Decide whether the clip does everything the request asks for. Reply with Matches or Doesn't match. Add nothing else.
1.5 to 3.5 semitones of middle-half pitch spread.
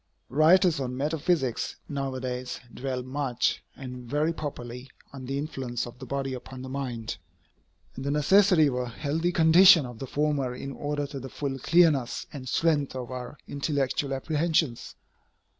Matches